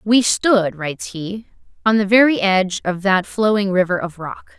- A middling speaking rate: Yes, average, 185 wpm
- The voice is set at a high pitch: Yes, high, 200 Hz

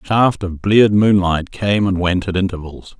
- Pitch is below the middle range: Yes, very low, 95 Hz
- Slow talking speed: No, average, 200 wpm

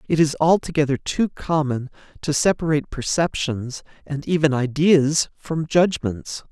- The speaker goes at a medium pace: No, slow, 120 wpm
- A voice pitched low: No, medium, 150 Hz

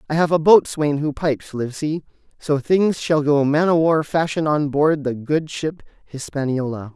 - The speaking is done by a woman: No, male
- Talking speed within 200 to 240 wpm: No, average, 175 wpm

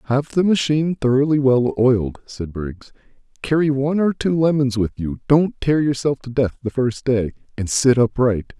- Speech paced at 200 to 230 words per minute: No, average, 180 wpm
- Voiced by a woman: No, male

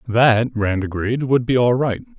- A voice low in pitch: Yes, low, 120 Hz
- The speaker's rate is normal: Yes, average, 190 wpm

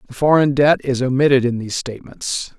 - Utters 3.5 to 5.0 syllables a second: No, 5.9 syllables/s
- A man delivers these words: Yes, male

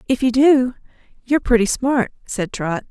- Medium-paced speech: Yes, average, 165 wpm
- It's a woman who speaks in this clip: Yes, female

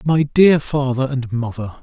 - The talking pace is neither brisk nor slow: Yes, average, 165 wpm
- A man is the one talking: Yes, male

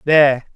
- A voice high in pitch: No, medium, 140 Hz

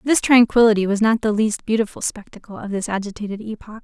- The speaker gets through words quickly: No, average, 190 wpm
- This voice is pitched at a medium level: No, high, 215 Hz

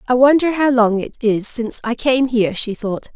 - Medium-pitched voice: No, high, 240 Hz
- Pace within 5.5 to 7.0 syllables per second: No, 5.2 syllables/s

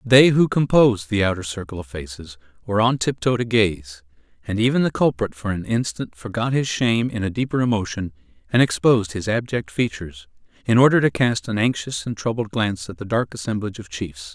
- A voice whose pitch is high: No, low, 110 Hz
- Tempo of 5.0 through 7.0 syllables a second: Yes, 5.8 syllables/s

